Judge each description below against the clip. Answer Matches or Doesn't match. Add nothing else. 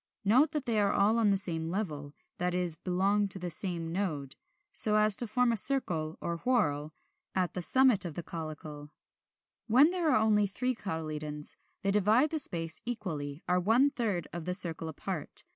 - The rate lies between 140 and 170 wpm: Doesn't match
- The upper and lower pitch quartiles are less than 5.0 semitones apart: Doesn't match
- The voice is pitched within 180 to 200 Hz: Matches